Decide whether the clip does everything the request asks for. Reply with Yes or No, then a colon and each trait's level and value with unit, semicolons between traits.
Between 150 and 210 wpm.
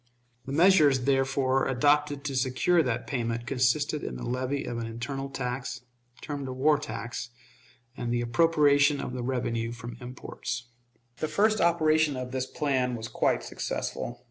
Yes: average, 155 wpm